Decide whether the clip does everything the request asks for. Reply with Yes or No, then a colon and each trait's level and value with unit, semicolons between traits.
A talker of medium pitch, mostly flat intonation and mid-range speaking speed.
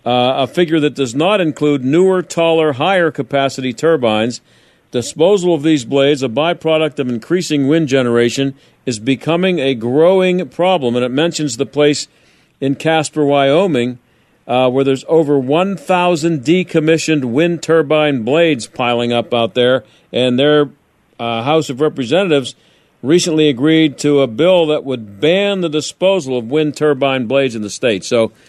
No: medium, 145 Hz; average, 3.9 semitones; average, 150 wpm